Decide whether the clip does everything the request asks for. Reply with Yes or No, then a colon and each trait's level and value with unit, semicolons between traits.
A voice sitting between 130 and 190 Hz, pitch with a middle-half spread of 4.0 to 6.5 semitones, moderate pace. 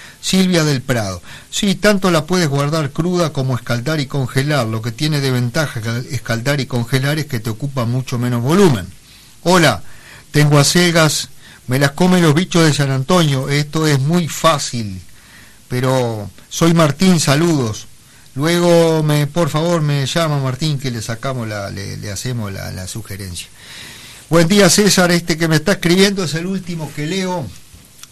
Yes: medium, 140 Hz; wide, 5.5 semitones; average, 165 wpm